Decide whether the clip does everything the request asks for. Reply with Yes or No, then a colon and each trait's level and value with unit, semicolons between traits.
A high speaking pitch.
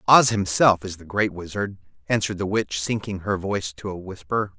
No: low, 100 Hz